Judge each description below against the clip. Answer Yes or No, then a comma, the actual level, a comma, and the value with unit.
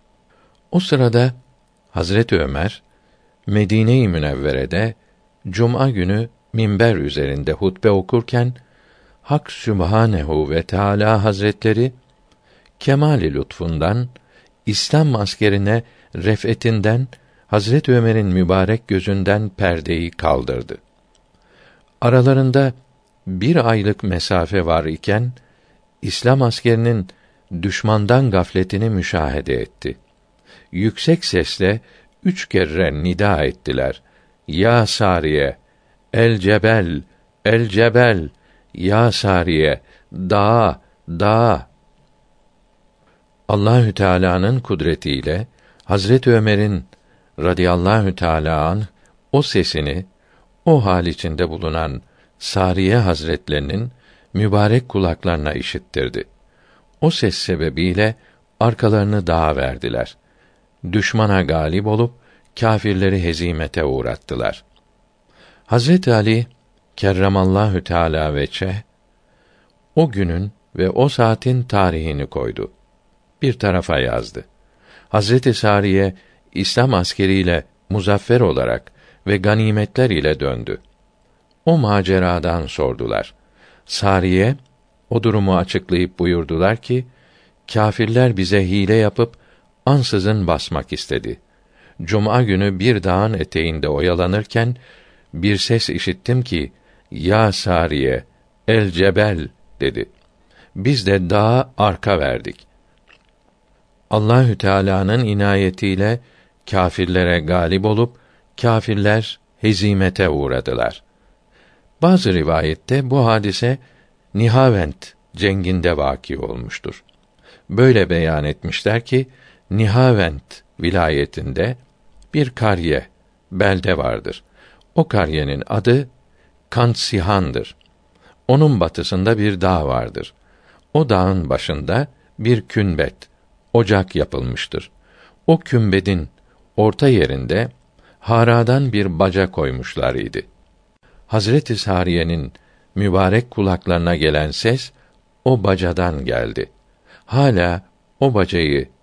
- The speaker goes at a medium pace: No, slow, 85 wpm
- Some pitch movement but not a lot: Yes, average, 4.9 semitones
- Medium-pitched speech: No, low, 100 Hz